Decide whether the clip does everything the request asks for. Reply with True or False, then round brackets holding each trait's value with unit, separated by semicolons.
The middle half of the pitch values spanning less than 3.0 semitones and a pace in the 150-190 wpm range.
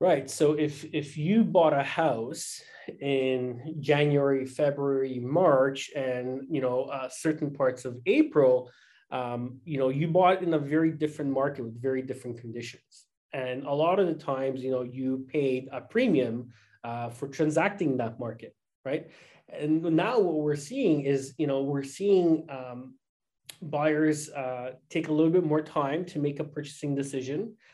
False (3.3 semitones; 165 wpm)